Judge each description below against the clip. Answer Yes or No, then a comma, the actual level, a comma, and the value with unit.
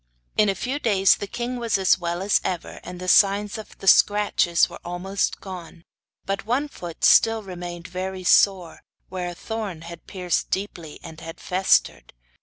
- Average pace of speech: Yes, average, 175 wpm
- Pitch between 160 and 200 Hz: Yes, high, 190 Hz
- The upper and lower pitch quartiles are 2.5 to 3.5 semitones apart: Yes, average, 2.8 semitones